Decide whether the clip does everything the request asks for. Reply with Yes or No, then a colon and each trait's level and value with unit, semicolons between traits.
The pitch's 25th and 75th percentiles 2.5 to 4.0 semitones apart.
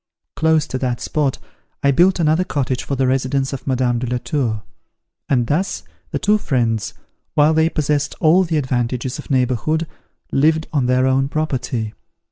Yes: average, 3.7 semitones